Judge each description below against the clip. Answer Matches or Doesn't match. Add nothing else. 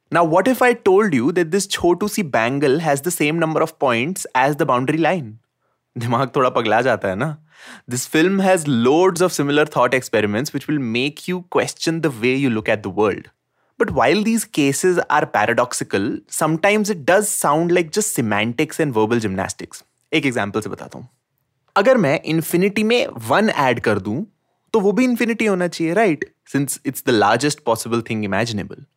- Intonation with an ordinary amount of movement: Doesn't match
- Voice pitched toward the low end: Doesn't match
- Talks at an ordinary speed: Matches